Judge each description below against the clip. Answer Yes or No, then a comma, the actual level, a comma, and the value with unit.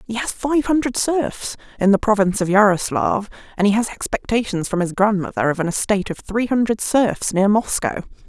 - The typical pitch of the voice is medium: No, high, 210 Hz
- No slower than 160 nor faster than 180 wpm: No, average, 190 wpm